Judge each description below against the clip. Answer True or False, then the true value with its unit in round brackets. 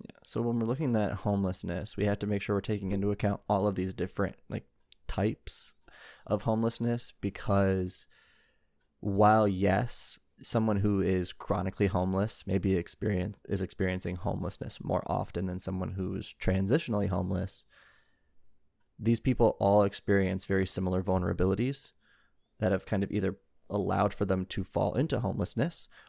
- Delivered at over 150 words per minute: False (145 wpm)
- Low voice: True (100 Hz)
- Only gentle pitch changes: True (2.1 semitones)